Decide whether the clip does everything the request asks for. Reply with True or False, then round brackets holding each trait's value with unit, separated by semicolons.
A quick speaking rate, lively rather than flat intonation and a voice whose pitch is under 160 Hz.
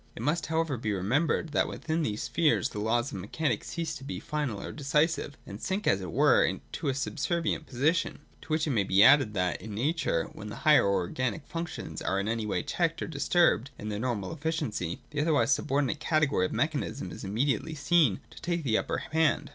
True (210 wpm; 6.9 semitones; 140 Hz)